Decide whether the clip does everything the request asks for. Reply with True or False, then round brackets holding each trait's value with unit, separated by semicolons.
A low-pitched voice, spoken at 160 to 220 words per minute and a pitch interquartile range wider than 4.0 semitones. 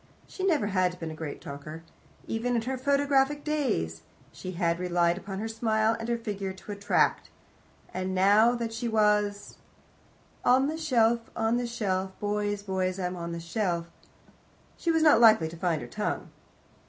False (210 Hz; 170 wpm; 4.5 semitones)